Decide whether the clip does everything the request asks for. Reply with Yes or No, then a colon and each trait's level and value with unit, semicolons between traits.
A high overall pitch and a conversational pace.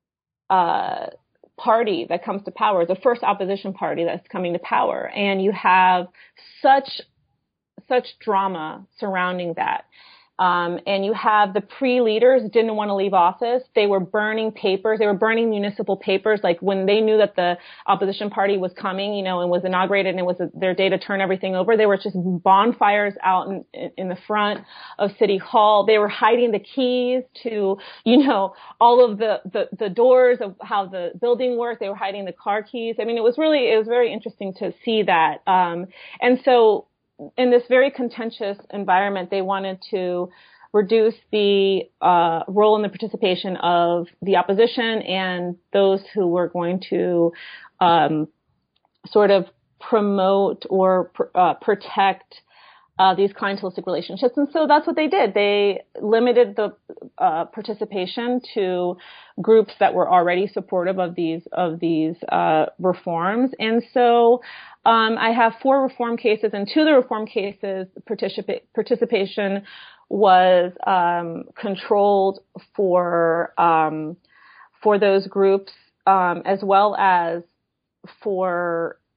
Yes: high, 200 Hz; average, 155 wpm